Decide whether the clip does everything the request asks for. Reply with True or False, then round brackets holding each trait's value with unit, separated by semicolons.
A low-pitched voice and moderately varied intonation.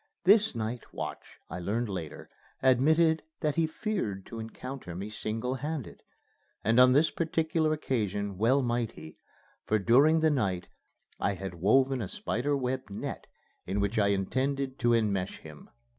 False (120 Hz; 5.7 semitones)